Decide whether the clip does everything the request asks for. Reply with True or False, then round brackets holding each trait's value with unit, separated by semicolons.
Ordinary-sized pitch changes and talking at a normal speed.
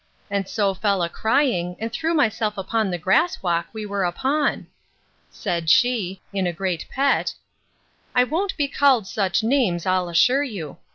False (6.2 semitones; 160 wpm)